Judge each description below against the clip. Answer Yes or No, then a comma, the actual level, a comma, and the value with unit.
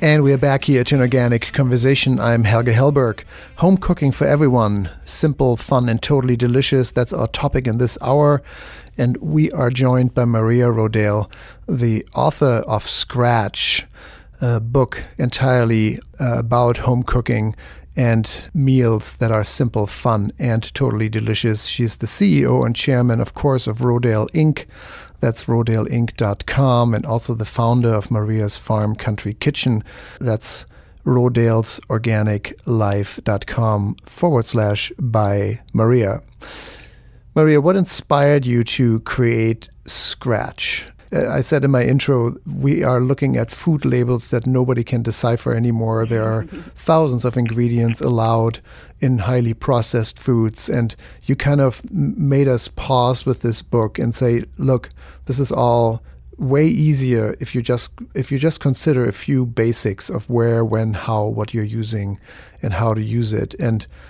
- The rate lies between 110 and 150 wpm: Yes, average, 145 wpm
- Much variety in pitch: No, average, 2.8 semitones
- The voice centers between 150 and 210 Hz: No, low, 120 Hz